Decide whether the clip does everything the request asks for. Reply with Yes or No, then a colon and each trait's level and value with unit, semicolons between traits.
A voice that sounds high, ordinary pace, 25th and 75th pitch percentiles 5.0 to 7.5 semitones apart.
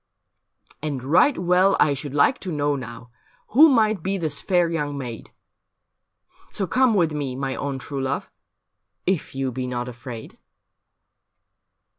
No: medium, 145 Hz; average, 150 wpm; wide, 5.6 semitones